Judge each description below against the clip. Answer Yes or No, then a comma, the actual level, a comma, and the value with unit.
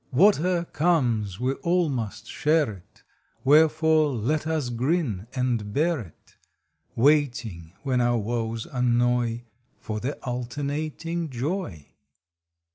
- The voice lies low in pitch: Yes, low, 130 Hz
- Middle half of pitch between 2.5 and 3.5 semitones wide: No, average, 5.1 semitones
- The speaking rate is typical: No, slow, 115 wpm